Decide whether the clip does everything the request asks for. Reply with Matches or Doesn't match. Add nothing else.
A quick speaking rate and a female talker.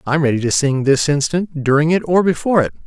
Doesn't match